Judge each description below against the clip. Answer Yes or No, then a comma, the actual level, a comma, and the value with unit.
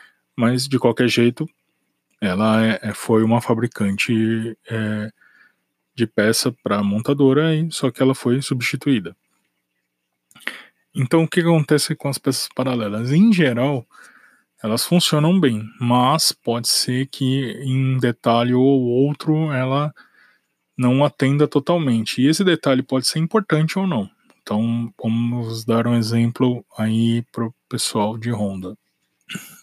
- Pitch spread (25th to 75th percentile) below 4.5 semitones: Yes, average, 3.9 semitones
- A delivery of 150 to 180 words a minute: No, average, 130 wpm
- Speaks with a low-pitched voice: Yes, low, 125 Hz